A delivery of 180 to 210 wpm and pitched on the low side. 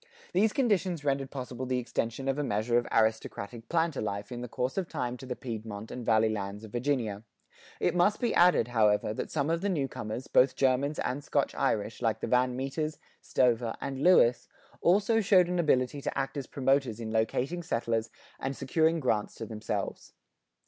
Yes: average, 185 wpm; low, 130 Hz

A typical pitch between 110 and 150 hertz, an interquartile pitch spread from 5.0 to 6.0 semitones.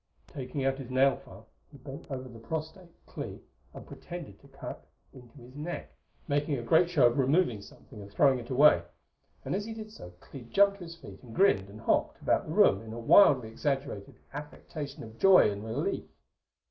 Yes: low, 135 Hz; average, 5.3 semitones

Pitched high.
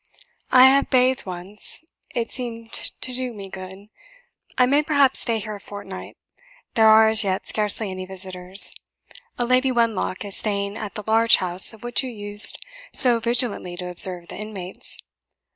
Yes: high, 215 Hz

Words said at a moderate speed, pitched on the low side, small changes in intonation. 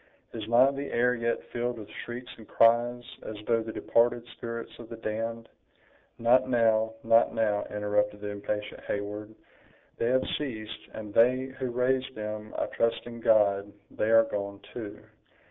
Yes: average, 160 wpm; low, 115 Hz; narrow, 2.2 semitones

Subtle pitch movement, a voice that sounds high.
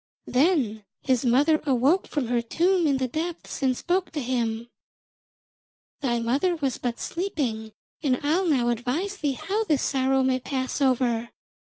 No: average, 4.6 semitones; very high, 265 Hz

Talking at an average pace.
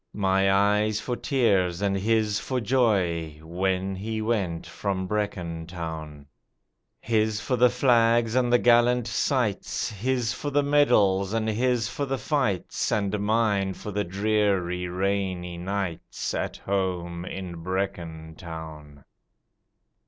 No: slow, 130 wpm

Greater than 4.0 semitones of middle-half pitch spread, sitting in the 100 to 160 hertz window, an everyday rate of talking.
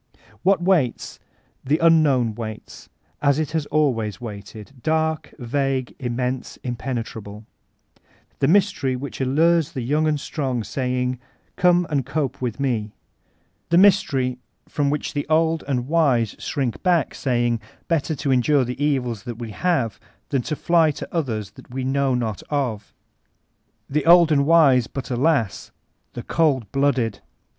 Yes: average, 4.4 semitones; low, 135 Hz; average, 145 wpm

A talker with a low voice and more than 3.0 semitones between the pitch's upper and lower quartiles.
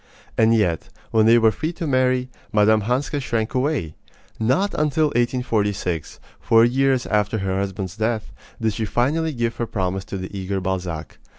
Yes: low, 110 Hz; average, 4.4 semitones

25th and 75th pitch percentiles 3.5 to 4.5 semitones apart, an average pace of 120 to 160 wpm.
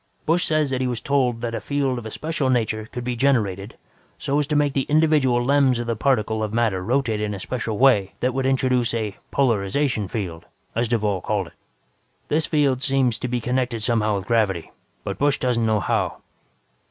No: average, 3.8 semitones; average, 200 wpm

